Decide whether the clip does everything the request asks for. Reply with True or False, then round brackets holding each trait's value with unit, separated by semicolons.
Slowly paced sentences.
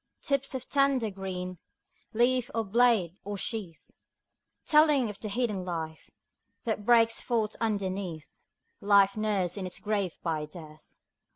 True (130 wpm)